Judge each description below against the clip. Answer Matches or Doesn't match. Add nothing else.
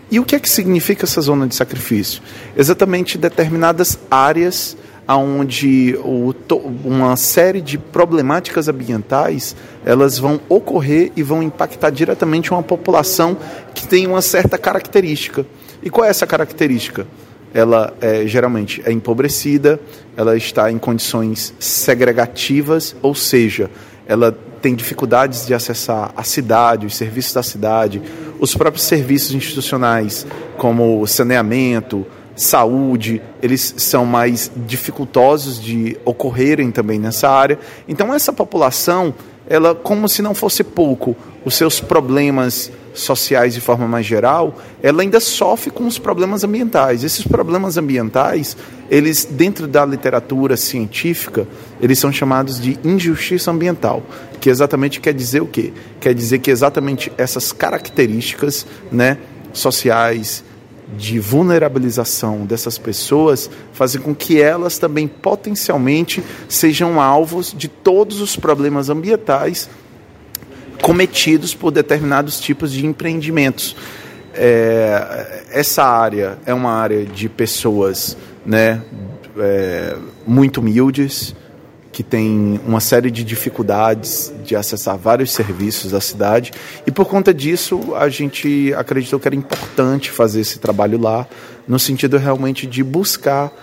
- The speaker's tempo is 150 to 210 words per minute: Doesn't match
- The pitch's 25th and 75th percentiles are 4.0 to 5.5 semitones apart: Matches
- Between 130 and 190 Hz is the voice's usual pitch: Matches